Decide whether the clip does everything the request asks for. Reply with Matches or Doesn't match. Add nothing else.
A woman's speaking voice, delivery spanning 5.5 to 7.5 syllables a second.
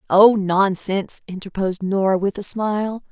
Doesn't match